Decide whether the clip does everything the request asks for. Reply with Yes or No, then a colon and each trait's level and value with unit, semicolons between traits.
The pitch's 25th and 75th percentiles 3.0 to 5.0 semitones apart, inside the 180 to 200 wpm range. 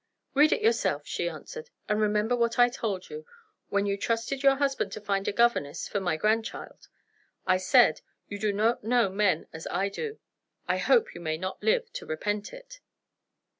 No: wide, 5.5 semitones; average, 185 wpm